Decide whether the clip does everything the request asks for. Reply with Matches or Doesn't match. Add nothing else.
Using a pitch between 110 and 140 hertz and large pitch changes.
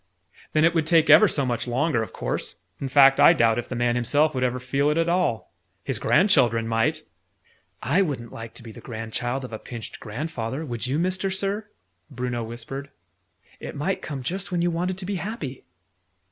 Matches